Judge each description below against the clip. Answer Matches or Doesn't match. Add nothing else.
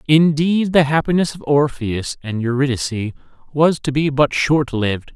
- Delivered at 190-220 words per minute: Doesn't match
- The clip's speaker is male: Matches